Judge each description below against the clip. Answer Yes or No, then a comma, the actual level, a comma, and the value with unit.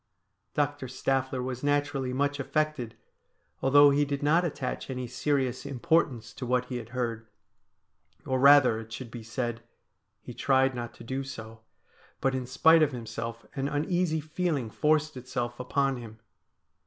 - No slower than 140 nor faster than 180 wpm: Yes, average, 155 wpm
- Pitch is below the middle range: Yes, low, 130 Hz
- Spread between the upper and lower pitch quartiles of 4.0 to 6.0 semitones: No, average, 3.0 semitones